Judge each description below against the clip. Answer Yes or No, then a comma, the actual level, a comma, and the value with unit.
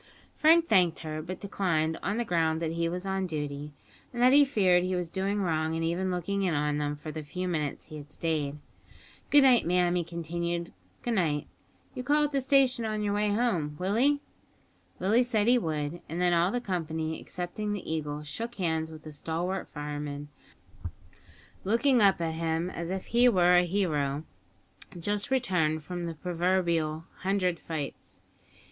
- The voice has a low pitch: No, medium, 175 Hz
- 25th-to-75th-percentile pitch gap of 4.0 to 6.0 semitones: Yes, average, 4.3 semitones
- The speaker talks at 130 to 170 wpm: No, average, 180 wpm